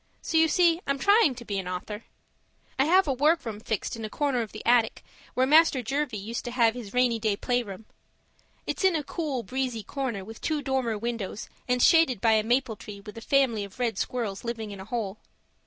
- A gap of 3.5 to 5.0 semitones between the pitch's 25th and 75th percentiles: Yes, average, 4.1 semitones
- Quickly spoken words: Yes, fast, 215 wpm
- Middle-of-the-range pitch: No, high, 240 Hz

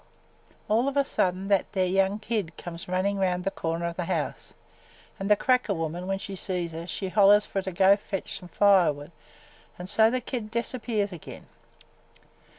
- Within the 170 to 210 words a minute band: Yes, average, 190 wpm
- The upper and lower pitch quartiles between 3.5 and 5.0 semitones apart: No, average, 2.8 semitones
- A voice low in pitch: No, high, 195 Hz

